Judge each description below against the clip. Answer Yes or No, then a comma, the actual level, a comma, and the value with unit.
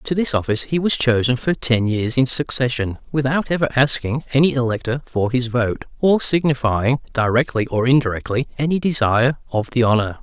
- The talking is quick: No, average, 170 wpm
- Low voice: Yes, low, 130 Hz